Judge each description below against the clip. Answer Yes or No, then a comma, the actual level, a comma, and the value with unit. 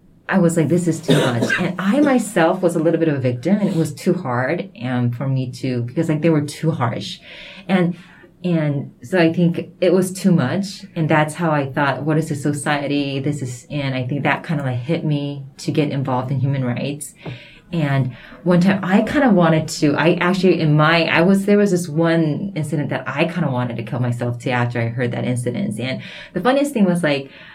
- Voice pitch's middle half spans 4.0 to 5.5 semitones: Yes, average, 4.4 semitones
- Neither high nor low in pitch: Yes, medium, 155 Hz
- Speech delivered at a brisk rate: Yes, fast, 225 wpm